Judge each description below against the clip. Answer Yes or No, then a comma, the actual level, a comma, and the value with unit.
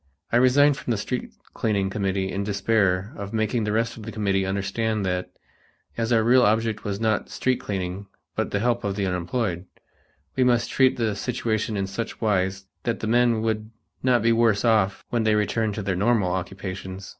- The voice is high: No, low, 110 Hz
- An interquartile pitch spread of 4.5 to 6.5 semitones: No, average, 2.9 semitones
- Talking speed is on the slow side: No, average, 190 wpm